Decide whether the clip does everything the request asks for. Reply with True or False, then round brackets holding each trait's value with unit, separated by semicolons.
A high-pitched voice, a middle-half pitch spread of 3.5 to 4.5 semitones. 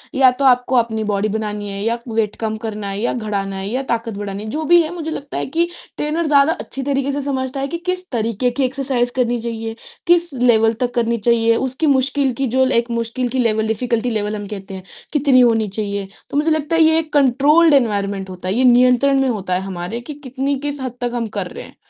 True (245 Hz; 4.1 semitones)